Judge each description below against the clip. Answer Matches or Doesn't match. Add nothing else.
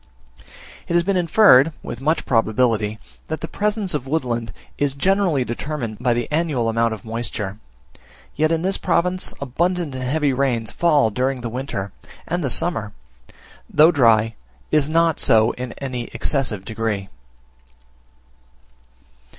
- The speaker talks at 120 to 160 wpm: Matches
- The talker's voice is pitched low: Matches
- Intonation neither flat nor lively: Doesn't match